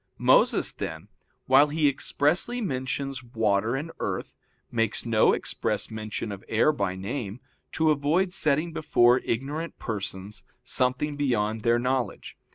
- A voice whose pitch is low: Yes, low, 130 Hz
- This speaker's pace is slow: Yes, slow, 130 wpm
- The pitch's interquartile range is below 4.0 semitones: No, average, 5.1 semitones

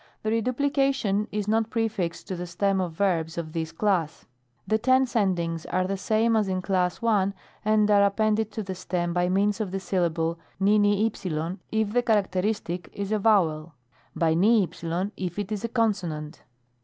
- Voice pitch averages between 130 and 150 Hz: No, high, 195 Hz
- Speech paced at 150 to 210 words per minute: Yes, average, 170 wpm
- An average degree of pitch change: Yes, average, 3.7 semitones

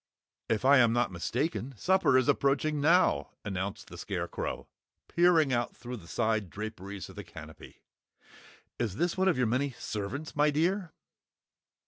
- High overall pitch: No, low, 125 Hz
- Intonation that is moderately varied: No, wide, 6.3 semitones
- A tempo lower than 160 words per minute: Yes, average, 150 wpm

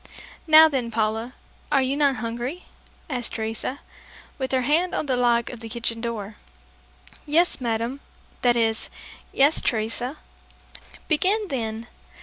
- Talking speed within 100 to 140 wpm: Yes, slow, 135 wpm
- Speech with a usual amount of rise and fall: Yes, average, 3.8 semitones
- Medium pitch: No, high, 245 Hz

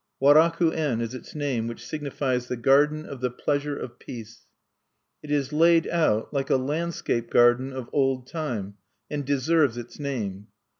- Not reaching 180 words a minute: Yes, average, 160 wpm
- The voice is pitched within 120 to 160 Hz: Yes, low, 135 Hz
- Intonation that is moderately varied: Yes, average, 3.7 semitones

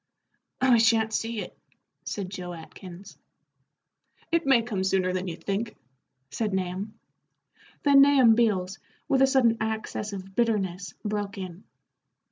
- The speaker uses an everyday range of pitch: Yes, average, 3.6 semitones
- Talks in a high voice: Yes, high, 210 Hz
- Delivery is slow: Yes, slow, 130 wpm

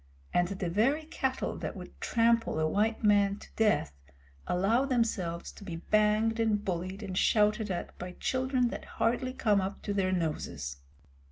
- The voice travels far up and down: No, average, 3.6 semitones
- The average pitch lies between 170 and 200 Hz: No, high, 210 Hz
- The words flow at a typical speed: Yes, average, 160 wpm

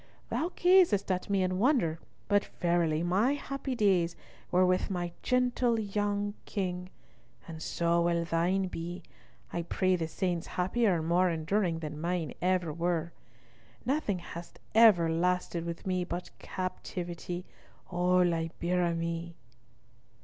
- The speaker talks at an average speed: No, slow, 130 wpm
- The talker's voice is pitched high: No, medium, 180 Hz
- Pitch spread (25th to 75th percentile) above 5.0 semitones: No, average, 2.7 semitones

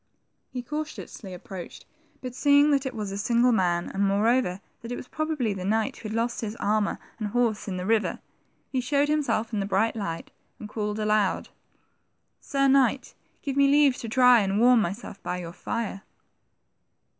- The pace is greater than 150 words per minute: Yes, average, 180 wpm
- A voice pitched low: No, high, 225 Hz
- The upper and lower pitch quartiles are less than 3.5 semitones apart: No, average, 4.2 semitones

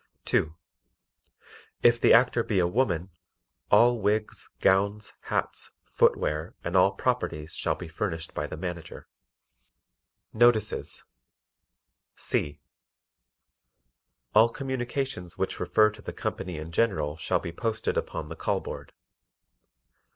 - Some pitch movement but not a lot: No, wide, 5.7 semitones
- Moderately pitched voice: No, low, 100 Hz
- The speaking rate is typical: No, slow, 115 wpm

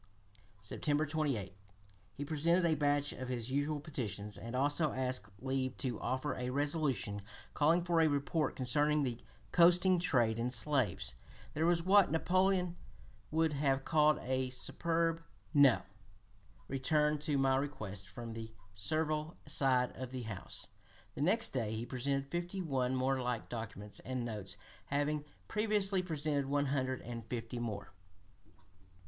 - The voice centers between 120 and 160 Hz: Yes, medium, 140 Hz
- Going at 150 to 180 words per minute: No, average, 140 wpm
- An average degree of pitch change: Yes, average, 3.9 semitones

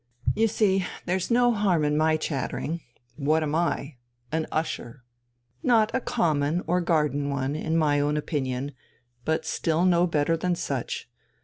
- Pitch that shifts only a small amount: No, average, 3.5 semitones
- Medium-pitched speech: Yes, medium, 160 Hz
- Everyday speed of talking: Yes, average, 150 wpm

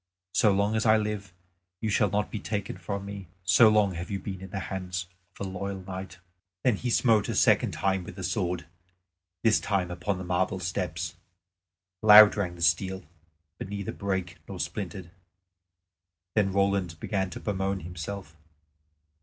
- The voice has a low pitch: Yes, very low, 95 Hz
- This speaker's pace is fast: No, average, 170 wpm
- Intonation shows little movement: Yes, narrow, 2.1 semitones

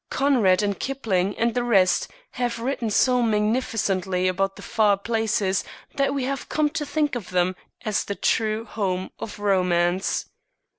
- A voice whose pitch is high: Yes, high, 215 Hz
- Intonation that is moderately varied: Yes, average, 4.4 semitones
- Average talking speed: Yes, average, 155 wpm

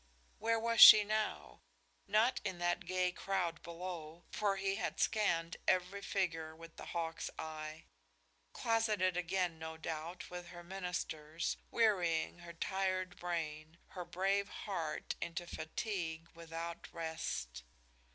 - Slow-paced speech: Yes, slow, 125 wpm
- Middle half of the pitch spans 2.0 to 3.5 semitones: Yes, average, 2.8 semitones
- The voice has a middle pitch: Yes, medium, 175 Hz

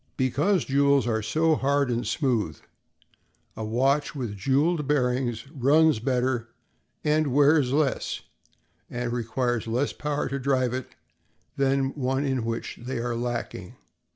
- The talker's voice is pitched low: Yes, low, 130 Hz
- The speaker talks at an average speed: No, slow, 130 wpm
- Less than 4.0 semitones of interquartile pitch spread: Yes, average, 2.8 semitones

